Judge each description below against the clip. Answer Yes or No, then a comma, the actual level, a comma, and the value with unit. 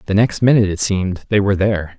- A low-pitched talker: Yes, low, 100 Hz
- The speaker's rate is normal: No, fast, 240 wpm